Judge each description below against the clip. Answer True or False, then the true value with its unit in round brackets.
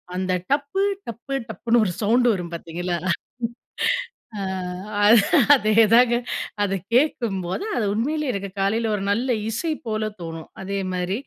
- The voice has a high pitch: True (215 Hz)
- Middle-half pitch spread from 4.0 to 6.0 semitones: True (4.3 semitones)